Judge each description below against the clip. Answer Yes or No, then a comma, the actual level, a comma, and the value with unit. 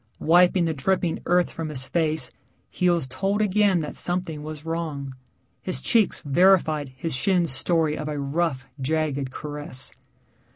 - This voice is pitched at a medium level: Yes, medium, 160 Hz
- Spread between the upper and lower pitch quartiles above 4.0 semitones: No, average, 3.4 semitones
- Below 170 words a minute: Yes, average, 150 wpm